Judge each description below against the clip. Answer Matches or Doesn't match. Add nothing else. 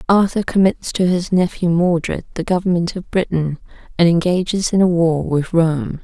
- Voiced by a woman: Matches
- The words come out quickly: Doesn't match